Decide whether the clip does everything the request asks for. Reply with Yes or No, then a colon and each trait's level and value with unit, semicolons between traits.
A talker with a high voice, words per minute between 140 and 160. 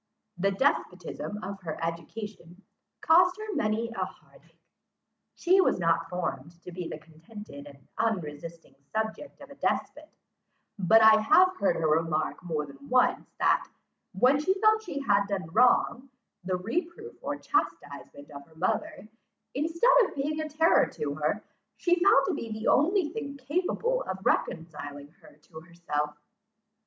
Yes: high, 205 Hz; average, 155 wpm